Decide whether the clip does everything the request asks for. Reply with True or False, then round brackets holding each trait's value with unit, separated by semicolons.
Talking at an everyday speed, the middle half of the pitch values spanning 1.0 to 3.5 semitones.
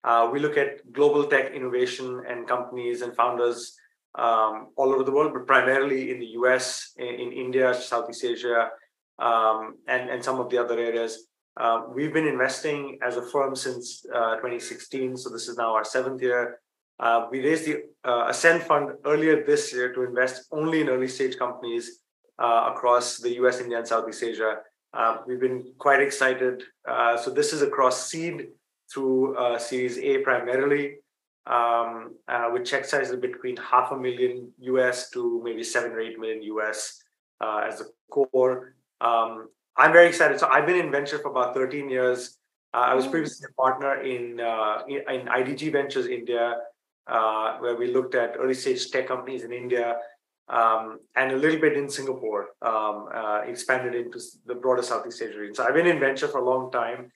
False (185 wpm; 3.0 semitones)